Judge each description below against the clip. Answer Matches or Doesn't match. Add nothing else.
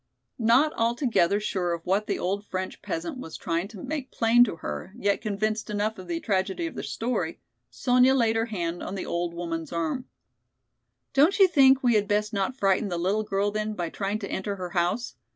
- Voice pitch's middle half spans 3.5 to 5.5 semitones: Matches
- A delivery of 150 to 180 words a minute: Doesn't match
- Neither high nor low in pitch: Doesn't match